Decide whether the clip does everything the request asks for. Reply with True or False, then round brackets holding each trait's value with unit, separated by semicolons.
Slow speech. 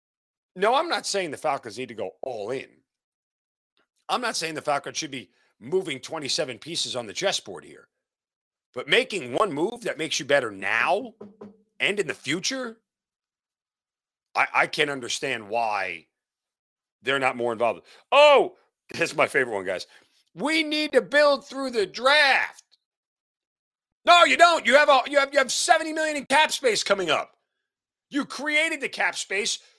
False (170 wpm)